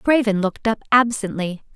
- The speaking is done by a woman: Yes, female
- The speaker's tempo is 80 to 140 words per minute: Yes, slow, 135 wpm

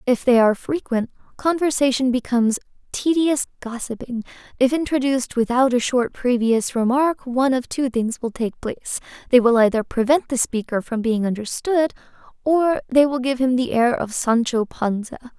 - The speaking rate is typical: Yes, average, 165 wpm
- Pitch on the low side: No, very high, 250 Hz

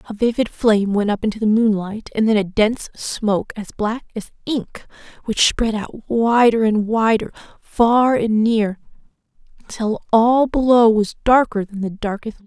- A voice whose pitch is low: No, high, 220 Hz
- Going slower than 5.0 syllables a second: Yes, 4.6 syllables/s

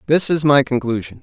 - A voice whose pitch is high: No, medium, 140 Hz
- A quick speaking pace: No, average, 195 wpm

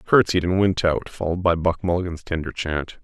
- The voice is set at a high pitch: No, very low, 90 Hz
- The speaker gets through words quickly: Yes, fast, 215 wpm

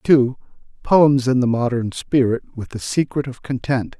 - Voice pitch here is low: Yes, low, 125 Hz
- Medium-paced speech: Yes, average, 165 wpm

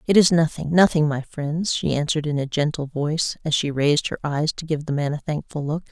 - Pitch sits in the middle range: Yes, medium, 150 Hz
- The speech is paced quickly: Yes, fast, 245 wpm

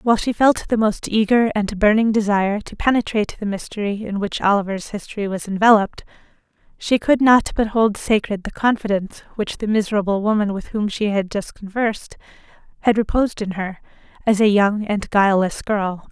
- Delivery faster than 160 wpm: Yes, average, 175 wpm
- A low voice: No, high, 210 Hz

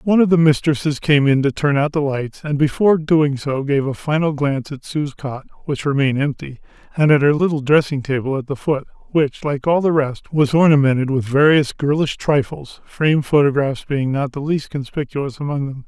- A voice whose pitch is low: No, medium, 145 Hz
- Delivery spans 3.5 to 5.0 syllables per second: No, 5.3 syllables/s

